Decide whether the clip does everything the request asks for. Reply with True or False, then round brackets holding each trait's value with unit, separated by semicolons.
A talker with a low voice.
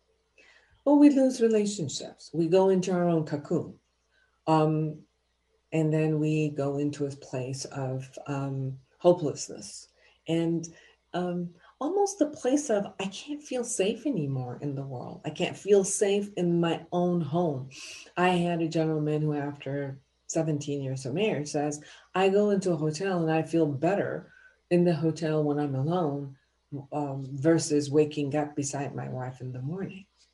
False (160 Hz)